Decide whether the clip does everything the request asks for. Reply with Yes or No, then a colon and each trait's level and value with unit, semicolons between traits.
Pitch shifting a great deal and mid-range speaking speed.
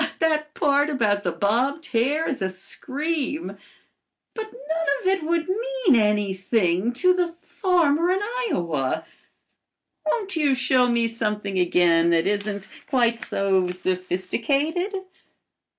No: wide, 8.6 semitones; slow, 120 wpm